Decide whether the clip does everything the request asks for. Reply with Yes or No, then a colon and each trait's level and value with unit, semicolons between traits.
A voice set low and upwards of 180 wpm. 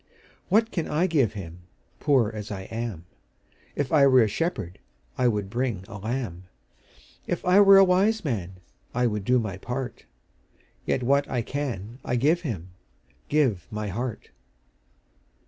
No: low, 120 Hz; average, 155 wpm